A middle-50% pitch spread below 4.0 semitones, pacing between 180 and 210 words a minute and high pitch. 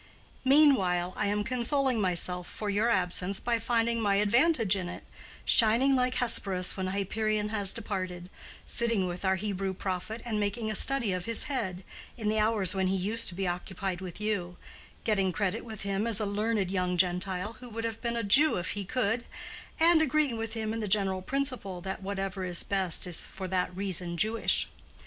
Yes: average, 3.6 semitones; average, 185 wpm; high, 205 Hz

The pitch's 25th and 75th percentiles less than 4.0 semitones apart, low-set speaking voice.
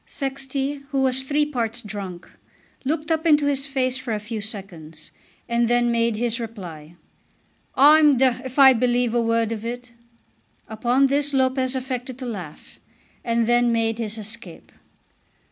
No: average, 3.0 semitones; high, 240 Hz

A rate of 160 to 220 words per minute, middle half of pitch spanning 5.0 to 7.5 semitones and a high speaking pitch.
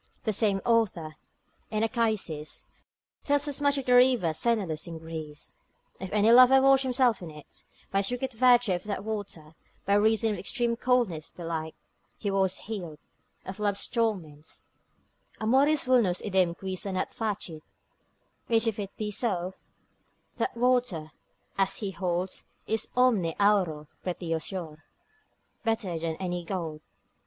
No: average, 145 wpm; average, 5.3 semitones; high, 200 Hz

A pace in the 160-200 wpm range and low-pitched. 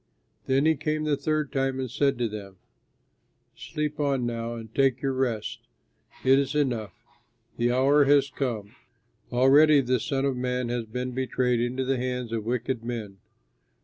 Yes: average, 165 wpm; low, 130 Hz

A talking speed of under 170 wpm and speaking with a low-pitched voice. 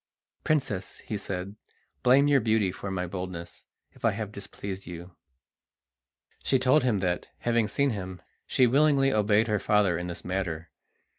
Yes: average, 155 wpm; low, 100 Hz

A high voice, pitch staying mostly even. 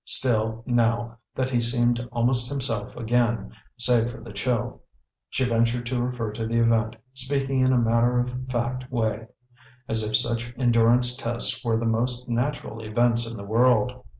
No: low, 120 Hz; narrow, 1.5 semitones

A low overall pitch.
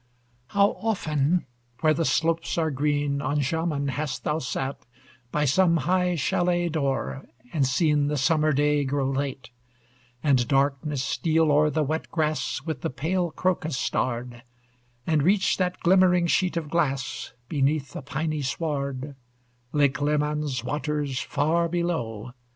No: medium, 150 Hz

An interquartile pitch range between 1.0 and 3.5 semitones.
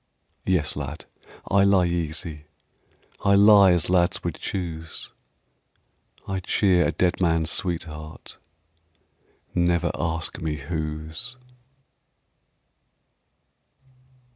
Yes: average, 3.0 semitones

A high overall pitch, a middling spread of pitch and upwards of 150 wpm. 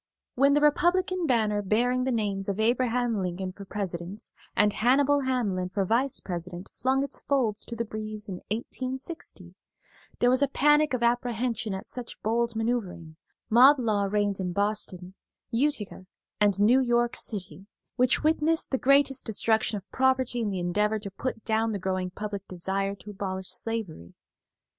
Yes: high, 220 Hz; average, 4.4 semitones; average, 160 wpm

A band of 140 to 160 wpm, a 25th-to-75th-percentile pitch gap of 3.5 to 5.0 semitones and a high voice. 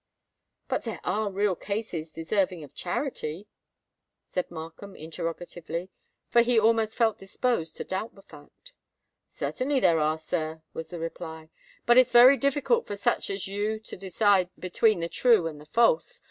No: average, 155 wpm; wide, 5.5 semitones; high, 195 Hz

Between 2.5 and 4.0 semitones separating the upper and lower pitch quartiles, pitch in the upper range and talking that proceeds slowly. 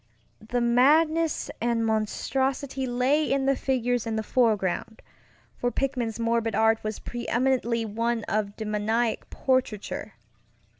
Yes: average, 2.9 semitones; high, 235 Hz; slow, 110 wpm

